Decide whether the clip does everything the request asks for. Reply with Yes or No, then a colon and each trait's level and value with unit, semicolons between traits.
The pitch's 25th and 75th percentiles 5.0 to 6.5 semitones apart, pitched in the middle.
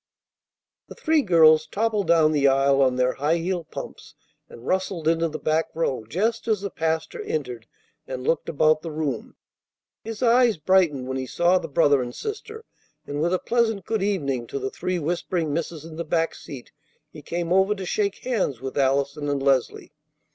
Yes: average, 5.3 semitones; medium, 160 Hz